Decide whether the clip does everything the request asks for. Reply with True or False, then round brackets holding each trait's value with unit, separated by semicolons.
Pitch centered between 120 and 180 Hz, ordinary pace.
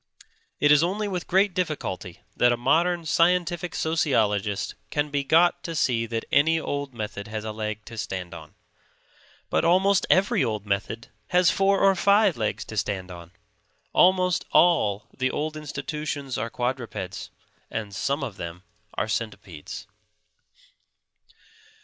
True (140 Hz; 145 wpm)